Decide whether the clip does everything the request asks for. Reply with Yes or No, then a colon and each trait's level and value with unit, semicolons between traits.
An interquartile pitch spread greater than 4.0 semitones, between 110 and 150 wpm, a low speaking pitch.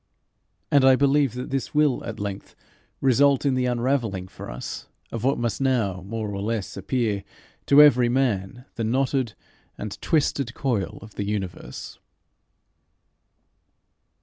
Yes: average, 4.6 semitones; average, 140 wpm; low, 120 Hz